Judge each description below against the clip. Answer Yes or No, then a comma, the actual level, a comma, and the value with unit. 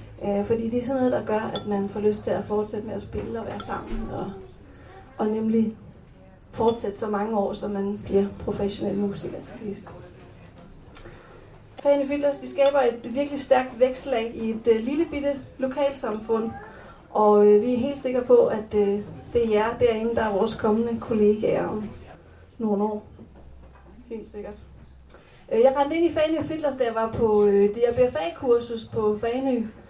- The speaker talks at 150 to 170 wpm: Yes, average, 165 wpm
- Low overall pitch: No, high, 225 Hz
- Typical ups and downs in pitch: Yes, average, 3.9 semitones